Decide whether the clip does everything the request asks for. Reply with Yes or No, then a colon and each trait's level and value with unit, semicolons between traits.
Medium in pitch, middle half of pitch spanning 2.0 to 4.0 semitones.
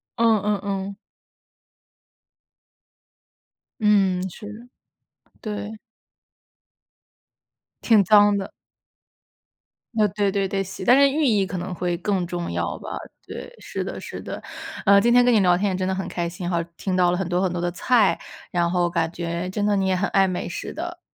No: high, 195 Hz; average, 2.7 semitones